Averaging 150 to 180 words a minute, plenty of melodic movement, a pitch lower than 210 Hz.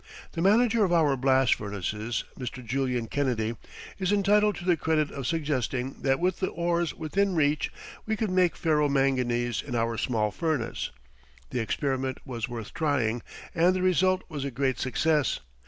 Yes: average, 165 wpm; wide, 6.0 semitones; medium, 140 Hz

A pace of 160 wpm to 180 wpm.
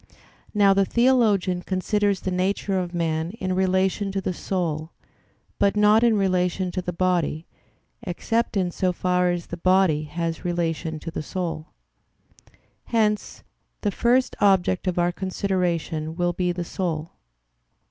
No: average, 145 wpm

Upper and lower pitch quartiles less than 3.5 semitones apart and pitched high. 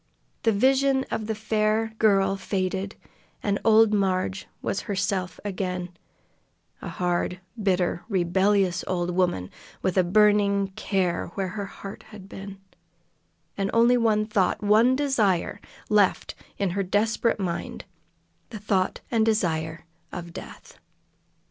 Yes: narrow, 2.5 semitones; high, 200 Hz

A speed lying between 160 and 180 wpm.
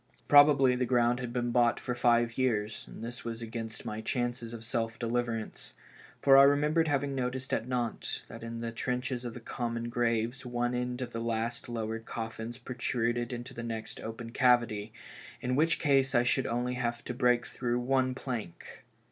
No: average, 190 wpm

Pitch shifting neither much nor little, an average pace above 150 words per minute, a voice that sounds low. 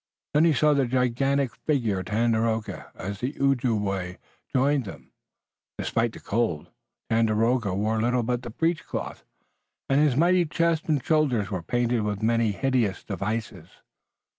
No: average, 4.3 semitones; average, 140 wpm; low, 120 Hz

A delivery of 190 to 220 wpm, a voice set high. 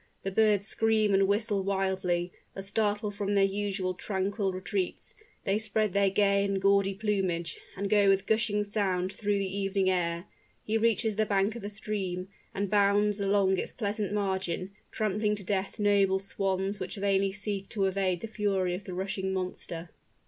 No: average, 170 wpm; high, 200 Hz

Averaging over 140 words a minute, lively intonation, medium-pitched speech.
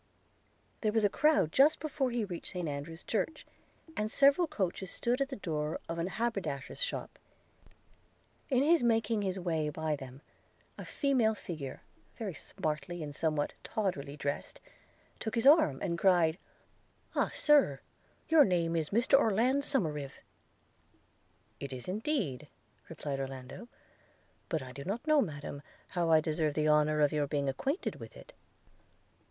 Yes: average, 150 wpm; wide, 7.8 semitones; medium, 175 Hz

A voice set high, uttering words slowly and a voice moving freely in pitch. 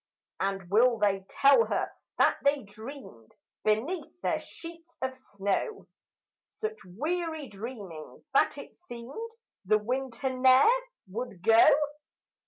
Yes: very high, 250 Hz; slow, 115 wpm; wide, 5.9 semitones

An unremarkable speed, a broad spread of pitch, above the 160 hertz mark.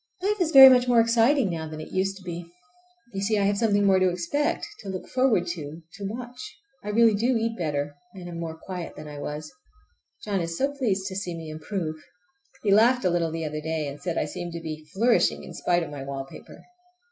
No: fast, 230 wpm; wide, 5.8 semitones; medium, 185 Hz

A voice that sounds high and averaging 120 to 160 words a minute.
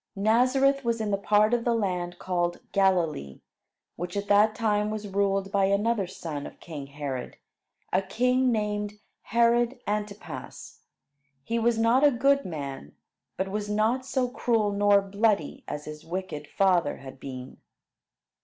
Yes: high, 205 Hz; average, 150 wpm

